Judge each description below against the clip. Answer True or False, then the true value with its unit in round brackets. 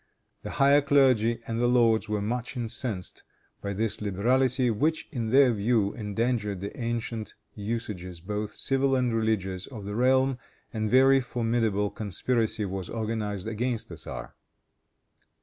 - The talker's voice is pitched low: True (115 Hz)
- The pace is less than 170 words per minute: True (145 wpm)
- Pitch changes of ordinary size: True (3.3 semitones)